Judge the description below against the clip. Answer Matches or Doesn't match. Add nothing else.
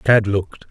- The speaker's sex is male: Matches